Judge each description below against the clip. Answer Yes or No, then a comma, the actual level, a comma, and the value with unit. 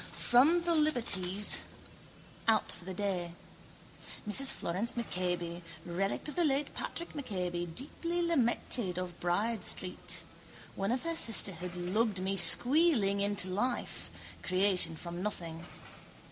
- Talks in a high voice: Yes, high, 200 Hz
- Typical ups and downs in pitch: No, wide, 5.8 semitones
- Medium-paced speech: No, slow, 120 wpm